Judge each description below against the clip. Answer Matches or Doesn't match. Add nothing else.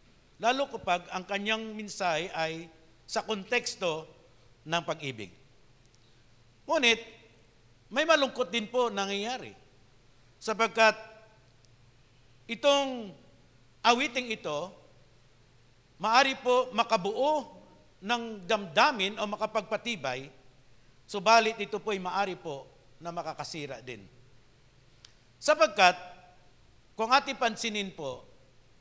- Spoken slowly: Matches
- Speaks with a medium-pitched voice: Matches